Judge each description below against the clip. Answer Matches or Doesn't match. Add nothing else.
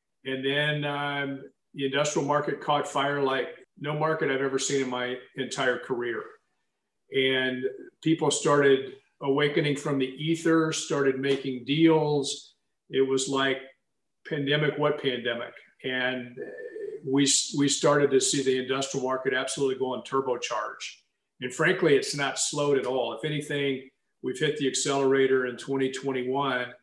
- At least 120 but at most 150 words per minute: Matches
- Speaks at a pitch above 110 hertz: Matches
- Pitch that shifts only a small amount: Matches